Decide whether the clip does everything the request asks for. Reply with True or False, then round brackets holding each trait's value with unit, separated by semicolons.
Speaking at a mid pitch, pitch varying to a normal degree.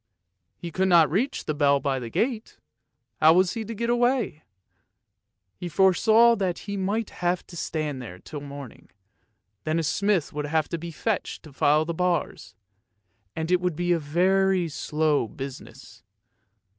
True (170 Hz; 4.3 semitones)